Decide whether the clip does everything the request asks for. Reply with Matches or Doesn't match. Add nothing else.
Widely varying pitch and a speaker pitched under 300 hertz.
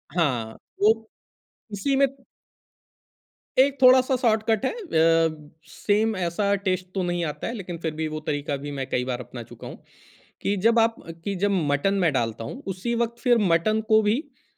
Matches